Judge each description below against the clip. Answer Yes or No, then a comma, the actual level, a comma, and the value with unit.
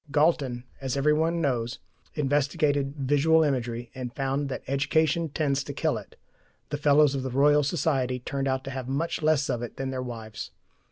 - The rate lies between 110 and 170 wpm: No, average, 180 wpm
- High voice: No, medium, 140 Hz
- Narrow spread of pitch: Yes, narrow, 2.3 semitones